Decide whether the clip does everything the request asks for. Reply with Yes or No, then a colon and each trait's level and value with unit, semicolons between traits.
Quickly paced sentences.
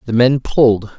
No: average, 185 wpm